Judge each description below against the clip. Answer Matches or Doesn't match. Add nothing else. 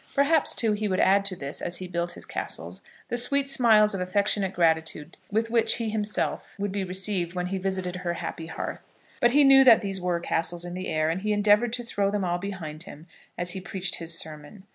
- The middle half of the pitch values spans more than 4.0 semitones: Doesn't match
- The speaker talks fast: Matches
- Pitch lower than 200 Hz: Matches